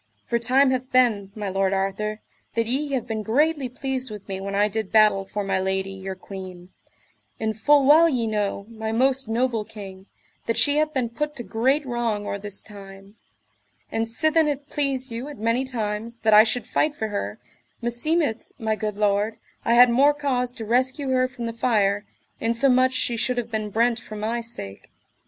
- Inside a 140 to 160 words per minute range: No, average, 190 wpm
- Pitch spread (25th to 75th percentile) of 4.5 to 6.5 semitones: No, average, 3.7 semitones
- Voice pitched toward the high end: Yes, high, 230 Hz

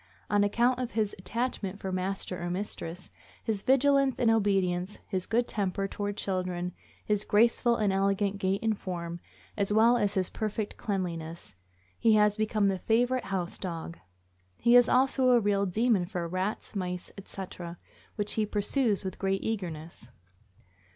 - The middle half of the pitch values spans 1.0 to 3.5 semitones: Yes, average, 3.2 semitones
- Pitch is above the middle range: Yes, high, 200 Hz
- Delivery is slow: No, average, 155 wpm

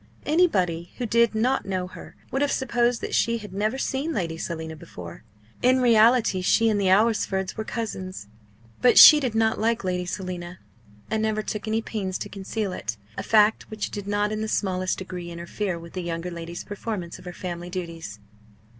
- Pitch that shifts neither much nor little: Yes, average, 4.0 semitones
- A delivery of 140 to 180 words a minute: No, average, 190 wpm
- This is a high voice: Yes, high, 205 Hz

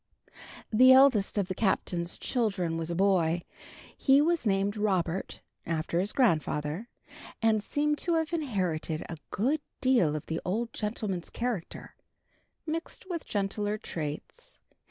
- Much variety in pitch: Yes, wide, 6.6 semitones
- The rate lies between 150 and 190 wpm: No, slow, 135 wpm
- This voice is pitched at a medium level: No, high, 205 Hz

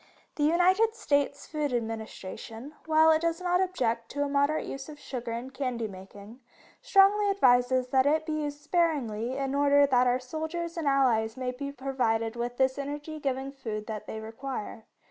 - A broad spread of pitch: No, average, 4.3 semitones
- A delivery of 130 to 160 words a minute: No, average, 175 wpm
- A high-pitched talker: Yes, very high, 275 Hz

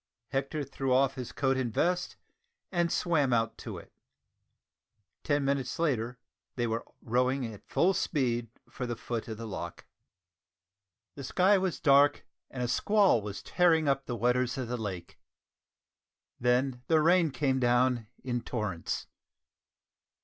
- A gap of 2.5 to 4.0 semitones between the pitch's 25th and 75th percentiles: Yes, average, 3.4 semitones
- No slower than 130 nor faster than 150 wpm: Yes, average, 145 wpm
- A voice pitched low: Yes, low, 130 Hz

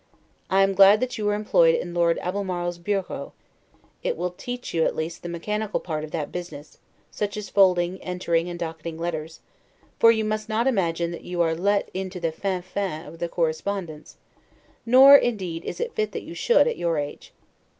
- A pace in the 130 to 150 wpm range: No, average, 190 wpm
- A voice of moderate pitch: Yes, medium, 180 Hz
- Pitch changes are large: No, average, 3.9 semitones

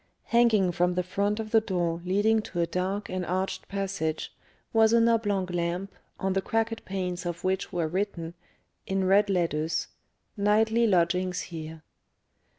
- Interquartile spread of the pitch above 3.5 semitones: No, average, 2.9 semitones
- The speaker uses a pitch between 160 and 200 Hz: Yes, high, 190 Hz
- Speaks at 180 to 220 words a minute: No, average, 155 wpm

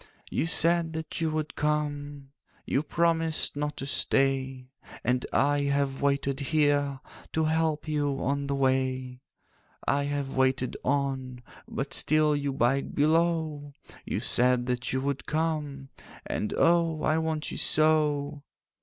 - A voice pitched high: No, medium, 145 Hz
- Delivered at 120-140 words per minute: Yes, slow, 135 wpm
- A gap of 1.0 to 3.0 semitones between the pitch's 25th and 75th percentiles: Yes, narrow, 2.4 semitones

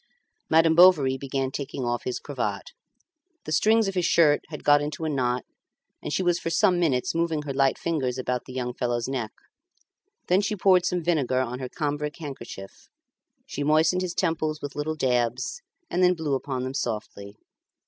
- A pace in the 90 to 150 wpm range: No, average, 180 wpm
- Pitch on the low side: No, medium, 145 Hz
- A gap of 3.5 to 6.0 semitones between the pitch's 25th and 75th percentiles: Yes, average, 4.5 semitones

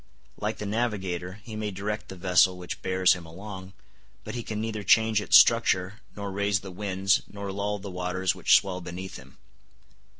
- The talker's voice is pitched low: Yes, very low, 95 Hz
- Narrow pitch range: Yes, narrow, 2.3 semitones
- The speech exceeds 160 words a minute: Yes, average, 180 wpm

